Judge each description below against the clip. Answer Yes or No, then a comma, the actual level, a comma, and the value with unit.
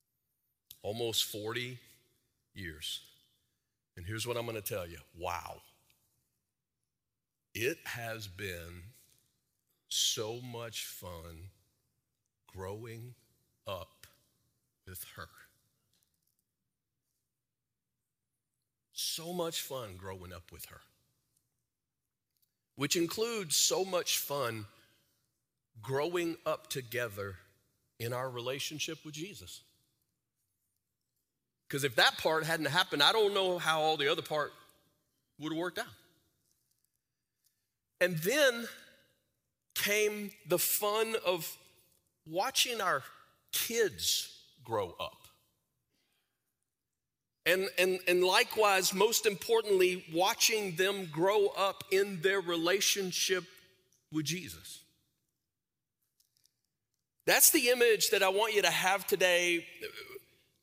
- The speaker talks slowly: Yes, slow, 95 wpm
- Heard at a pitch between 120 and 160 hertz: Yes, low, 135 Hz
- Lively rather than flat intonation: Yes, wide, 7.9 semitones